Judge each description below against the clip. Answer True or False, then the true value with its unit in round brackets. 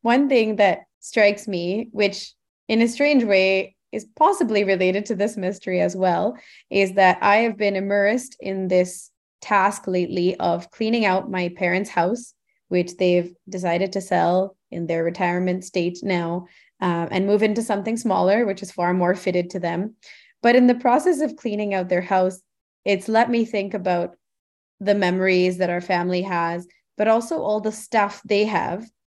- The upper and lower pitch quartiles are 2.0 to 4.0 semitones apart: True (3.0 semitones)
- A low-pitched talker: False (195 Hz)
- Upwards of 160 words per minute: True (175 wpm)